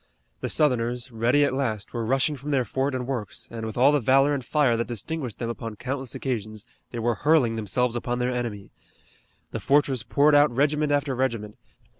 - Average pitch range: Yes, average, 3.4 semitones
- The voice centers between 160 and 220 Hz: No, low, 125 Hz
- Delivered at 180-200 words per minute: Yes, average, 195 wpm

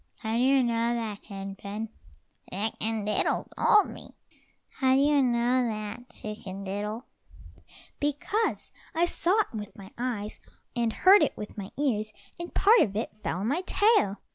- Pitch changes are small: No, average, 4.7 semitones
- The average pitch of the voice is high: Yes, high, 230 Hz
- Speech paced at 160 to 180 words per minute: Yes, average, 165 wpm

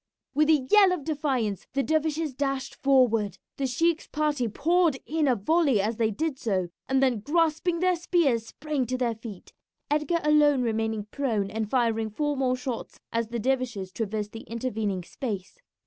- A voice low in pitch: No, very high, 260 Hz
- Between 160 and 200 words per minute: Yes, average, 170 wpm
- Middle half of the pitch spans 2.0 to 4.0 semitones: No, average, 5.3 semitones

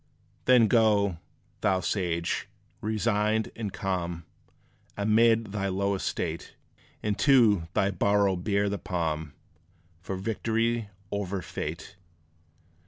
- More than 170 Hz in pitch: No, low, 100 Hz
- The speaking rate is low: Yes, slow, 105 wpm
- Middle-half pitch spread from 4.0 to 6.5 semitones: No, average, 2.8 semitones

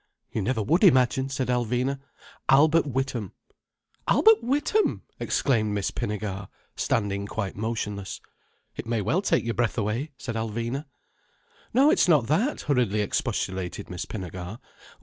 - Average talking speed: No, slow, 130 wpm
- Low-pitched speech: Yes, low, 115 Hz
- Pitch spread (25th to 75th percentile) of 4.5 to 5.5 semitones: Yes, average, 5.2 semitones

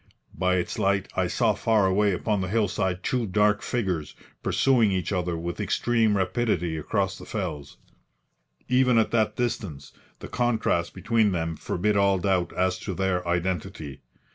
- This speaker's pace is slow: No, average, 155 wpm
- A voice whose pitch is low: Yes, very low, 95 Hz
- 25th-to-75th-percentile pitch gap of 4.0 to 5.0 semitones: No, average, 3.4 semitones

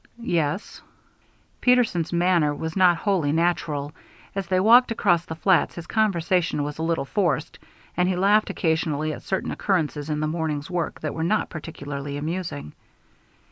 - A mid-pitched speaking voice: Yes, medium, 170 Hz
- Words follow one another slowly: No, average, 155 wpm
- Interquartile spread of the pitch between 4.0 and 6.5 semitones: No, average, 3.5 semitones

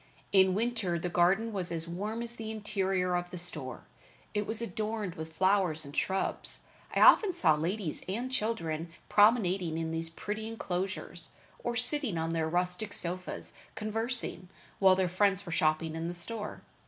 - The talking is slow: No, average, 165 wpm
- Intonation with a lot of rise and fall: No, average, 4.1 semitones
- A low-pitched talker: No, medium, 185 Hz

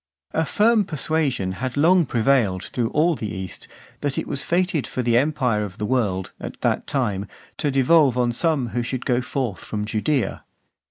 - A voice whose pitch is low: Yes, low, 130 Hz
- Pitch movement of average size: No, wide, 5.8 semitones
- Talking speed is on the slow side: No, average, 180 wpm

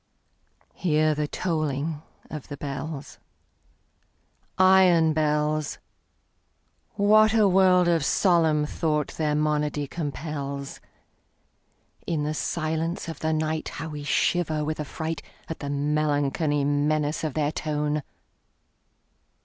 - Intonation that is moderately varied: No, narrow, 1.7 semitones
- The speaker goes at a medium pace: No, slow, 95 wpm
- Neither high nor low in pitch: Yes, medium, 155 Hz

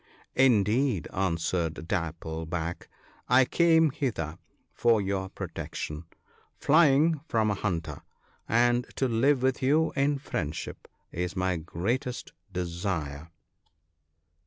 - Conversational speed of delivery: No, slow, 110 wpm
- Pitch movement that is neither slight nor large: No, wide, 7.8 semitones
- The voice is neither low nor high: No, low, 100 Hz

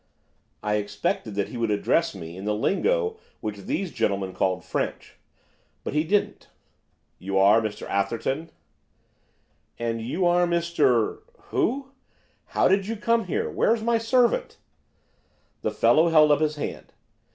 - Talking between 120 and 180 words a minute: Yes, average, 140 wpm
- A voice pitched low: No, medium, 150 Hz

